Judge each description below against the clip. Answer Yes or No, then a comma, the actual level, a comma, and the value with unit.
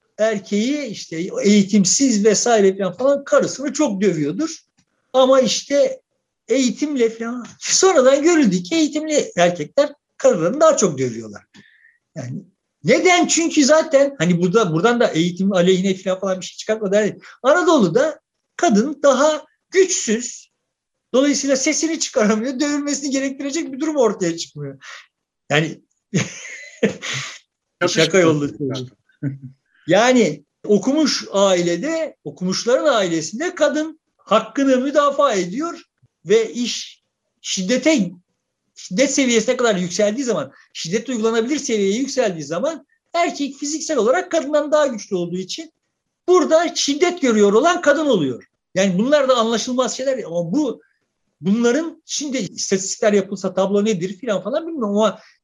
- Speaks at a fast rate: No, average, 115 wpm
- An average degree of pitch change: No, wide, 7.3 semitones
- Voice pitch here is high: Yes, high, 245 Hz